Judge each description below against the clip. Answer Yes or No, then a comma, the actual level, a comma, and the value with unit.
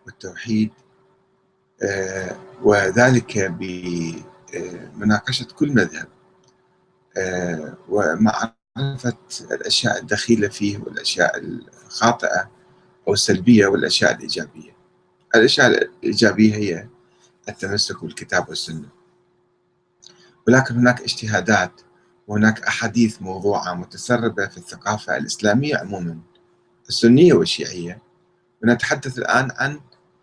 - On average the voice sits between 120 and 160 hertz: No, low, 110 Hz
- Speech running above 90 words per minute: No, average, 75 wpm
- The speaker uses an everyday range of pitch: Yes, average, 4.7 semitones